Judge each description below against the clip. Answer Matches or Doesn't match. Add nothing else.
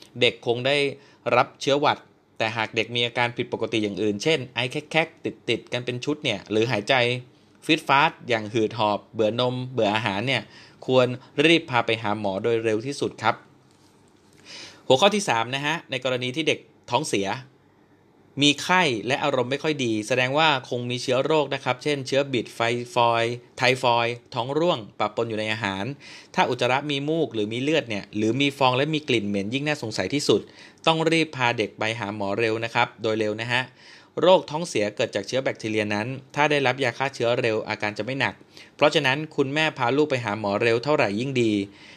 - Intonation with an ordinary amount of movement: Matches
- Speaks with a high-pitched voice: Doesn't match